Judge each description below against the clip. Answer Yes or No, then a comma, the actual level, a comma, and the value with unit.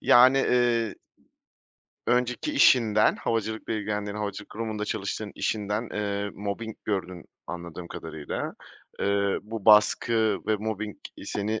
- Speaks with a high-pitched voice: No, low, 105 Hz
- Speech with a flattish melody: Yes, narrow, 1.8 semitones